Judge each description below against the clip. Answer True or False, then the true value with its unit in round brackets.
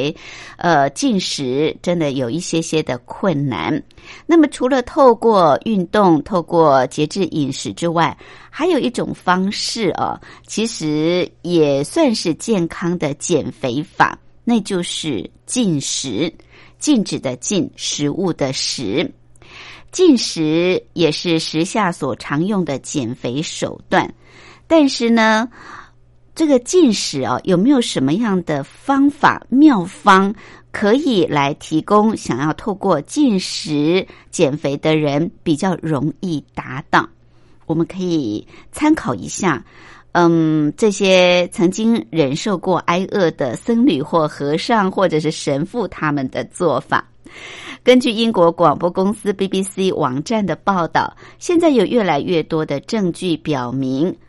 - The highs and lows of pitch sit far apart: True (5.9 semitones)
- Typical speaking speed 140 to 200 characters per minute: True (195 characters per minute)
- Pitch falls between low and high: True (175 Hz)